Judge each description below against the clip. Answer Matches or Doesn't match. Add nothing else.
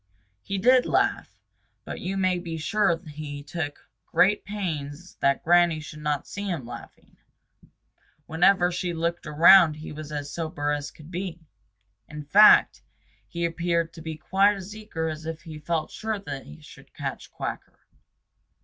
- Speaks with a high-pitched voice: Doesn't match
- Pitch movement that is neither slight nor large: Matches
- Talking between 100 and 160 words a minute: Matches